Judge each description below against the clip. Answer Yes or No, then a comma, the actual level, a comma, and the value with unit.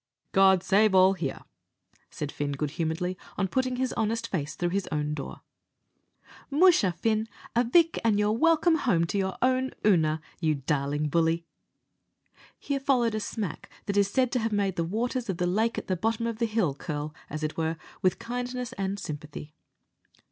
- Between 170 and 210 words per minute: Yes, average, 175 wpm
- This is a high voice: Yes, high, 195 Hz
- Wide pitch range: Yes, wide, 6.1 semitones